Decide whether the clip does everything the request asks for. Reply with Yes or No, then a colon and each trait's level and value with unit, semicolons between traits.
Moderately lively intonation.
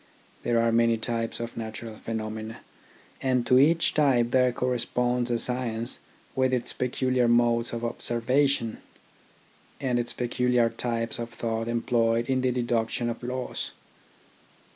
No: narrow, 1.6 semitones